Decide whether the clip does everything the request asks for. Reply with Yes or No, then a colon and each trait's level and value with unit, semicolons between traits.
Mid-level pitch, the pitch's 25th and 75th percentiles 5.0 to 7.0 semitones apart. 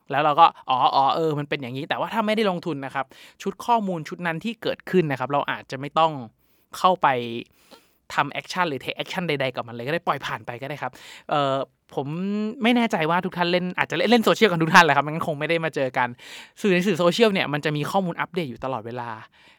Yes: medium, 160 Hz; average, 5.3 semitones